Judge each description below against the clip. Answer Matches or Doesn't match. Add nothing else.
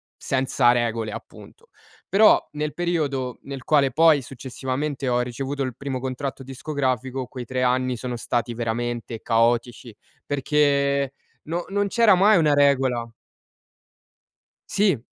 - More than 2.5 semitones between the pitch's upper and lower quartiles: Matches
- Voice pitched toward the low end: Matches